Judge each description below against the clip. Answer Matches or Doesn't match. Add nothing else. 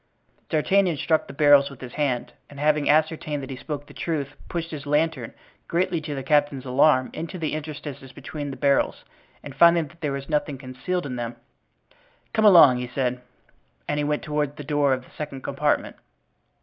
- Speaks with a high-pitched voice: Doesn't match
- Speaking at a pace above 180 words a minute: Matches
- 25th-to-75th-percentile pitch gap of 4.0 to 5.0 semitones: Doesn't match